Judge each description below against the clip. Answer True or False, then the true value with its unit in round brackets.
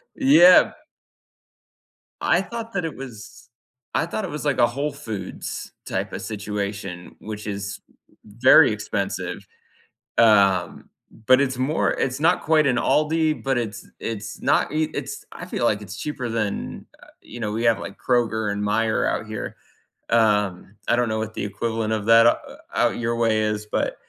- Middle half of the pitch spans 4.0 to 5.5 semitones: True (4.5 semitones)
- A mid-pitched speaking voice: False (115 Hz)